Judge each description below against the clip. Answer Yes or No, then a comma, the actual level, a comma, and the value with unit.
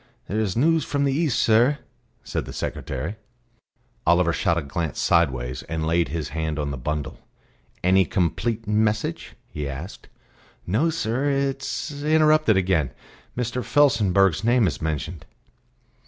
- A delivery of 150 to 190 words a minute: No, average, 140 wpm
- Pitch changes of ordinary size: No, wide, 8.0 semitones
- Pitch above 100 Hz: No, very low, 95 Hz